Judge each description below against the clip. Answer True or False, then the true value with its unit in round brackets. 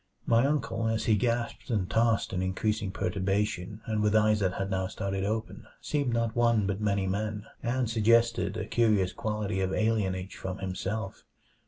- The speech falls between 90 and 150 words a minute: False (170 wpm)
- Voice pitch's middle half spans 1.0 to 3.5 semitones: True (2.8 semitones)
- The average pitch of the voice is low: True (105 Hz)